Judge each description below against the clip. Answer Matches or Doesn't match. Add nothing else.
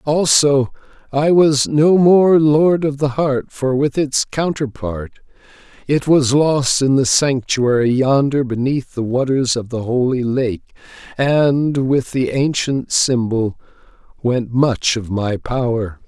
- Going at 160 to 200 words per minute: Doesn't match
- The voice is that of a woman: Doesn't match